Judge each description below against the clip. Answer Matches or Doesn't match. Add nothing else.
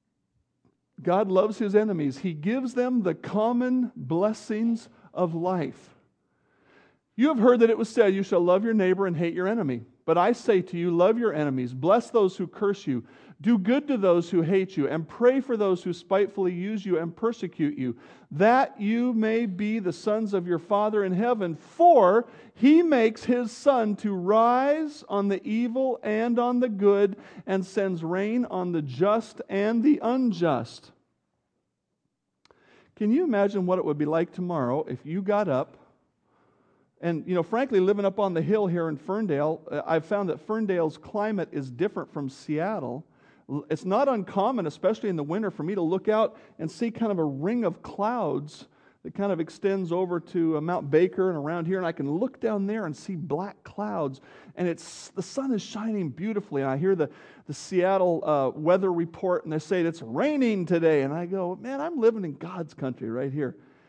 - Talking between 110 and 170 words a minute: Doesn't match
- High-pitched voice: Matches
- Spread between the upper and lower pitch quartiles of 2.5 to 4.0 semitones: Doesn't match